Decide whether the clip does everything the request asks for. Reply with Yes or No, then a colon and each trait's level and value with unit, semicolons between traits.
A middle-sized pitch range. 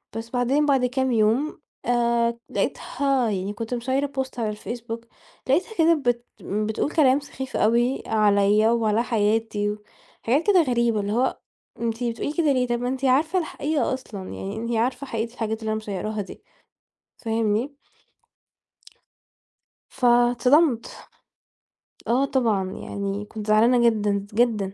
Yes: average, 3.3 semitones